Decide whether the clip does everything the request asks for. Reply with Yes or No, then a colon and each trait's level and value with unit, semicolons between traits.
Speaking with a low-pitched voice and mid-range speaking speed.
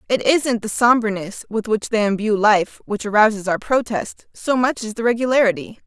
No: high, 220 Hz; average, 185 wpm